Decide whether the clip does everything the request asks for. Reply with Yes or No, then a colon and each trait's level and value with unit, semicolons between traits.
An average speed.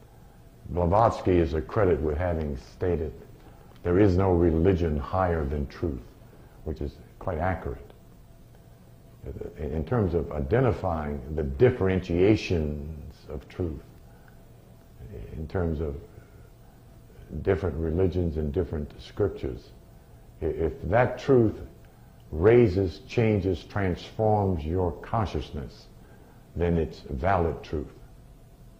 No: slow, 95 wpm